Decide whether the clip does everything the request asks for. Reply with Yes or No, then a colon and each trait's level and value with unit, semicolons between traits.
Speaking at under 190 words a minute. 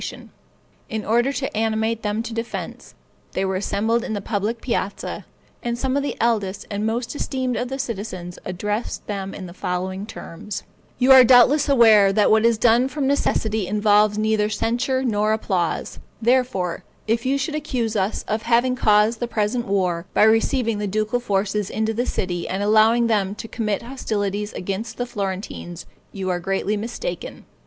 Yes: average, 170 wpm